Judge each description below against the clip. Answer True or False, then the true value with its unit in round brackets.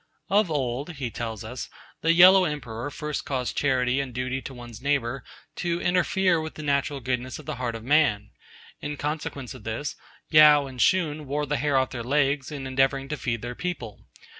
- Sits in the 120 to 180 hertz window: True (135 Hz)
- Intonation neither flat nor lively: True (3.2 semitones)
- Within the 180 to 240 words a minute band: True (190 wpm)